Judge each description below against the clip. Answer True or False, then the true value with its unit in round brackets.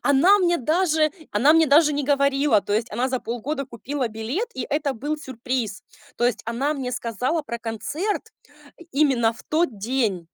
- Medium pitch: False (265 Hz)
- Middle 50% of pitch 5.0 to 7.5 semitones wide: False (4.6 semitones)